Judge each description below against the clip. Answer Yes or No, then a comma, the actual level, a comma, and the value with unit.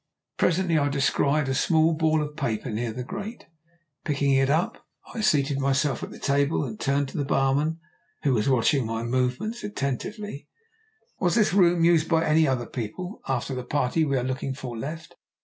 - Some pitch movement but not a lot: Yes, average, 3.7 semitones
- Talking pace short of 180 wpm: No, average, 185 wpm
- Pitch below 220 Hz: Yes, medium, 140 Hz